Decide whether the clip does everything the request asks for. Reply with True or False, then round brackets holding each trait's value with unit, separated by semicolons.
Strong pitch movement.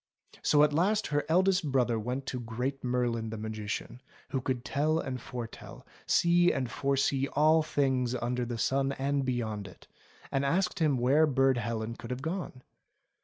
False (3.4 semitones)